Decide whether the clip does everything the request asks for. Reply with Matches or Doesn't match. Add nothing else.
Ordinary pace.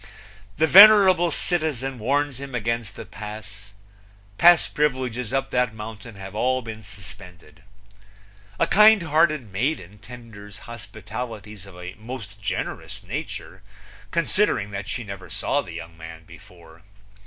Doesn't match